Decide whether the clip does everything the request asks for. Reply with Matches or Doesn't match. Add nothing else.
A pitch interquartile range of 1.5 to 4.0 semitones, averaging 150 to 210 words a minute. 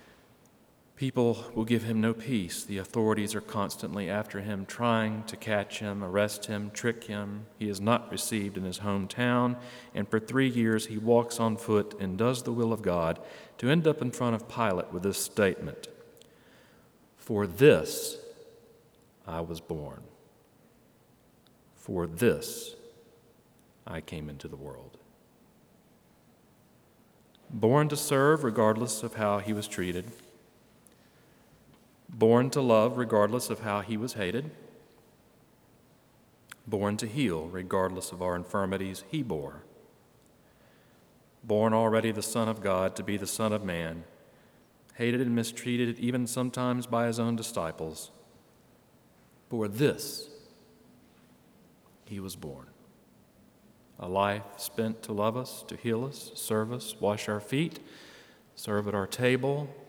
Doesn't match